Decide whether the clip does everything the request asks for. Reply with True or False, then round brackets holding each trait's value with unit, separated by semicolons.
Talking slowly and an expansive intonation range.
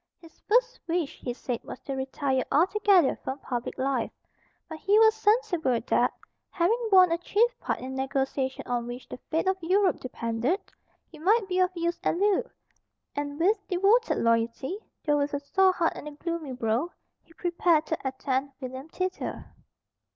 False (175 wpm; 6.2 semitones)